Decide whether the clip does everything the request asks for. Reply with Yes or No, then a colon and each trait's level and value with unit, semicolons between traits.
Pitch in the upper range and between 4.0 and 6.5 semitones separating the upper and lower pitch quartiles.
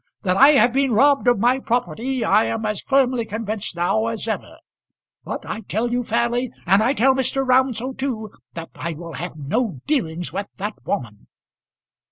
Yes: high, 225 Hz; average, 4.3 semitones